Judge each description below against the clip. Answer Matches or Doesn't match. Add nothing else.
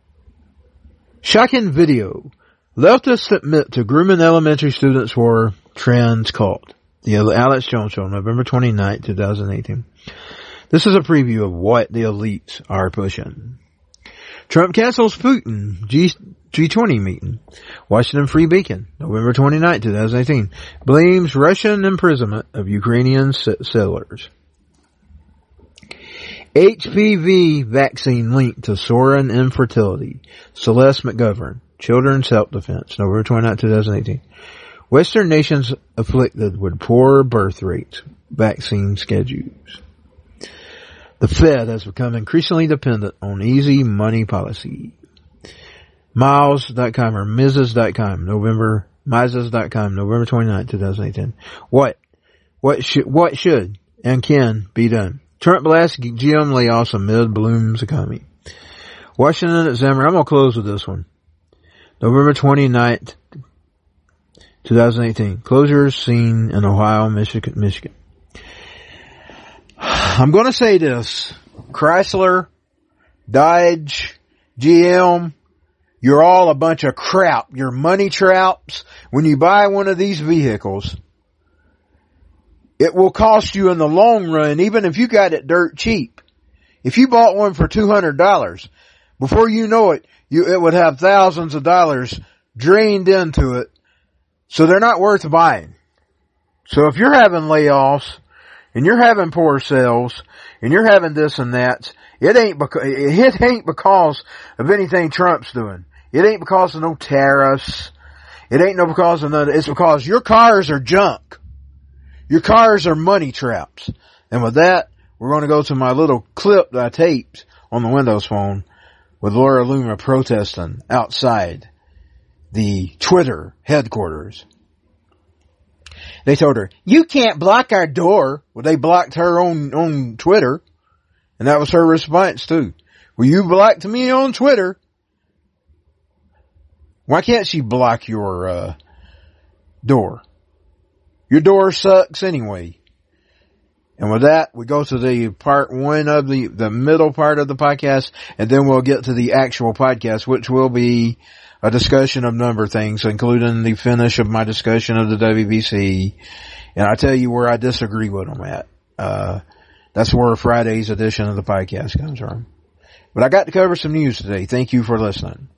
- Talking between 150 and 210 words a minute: Doesn't match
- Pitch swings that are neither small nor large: Doesn't match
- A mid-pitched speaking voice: Doesn't match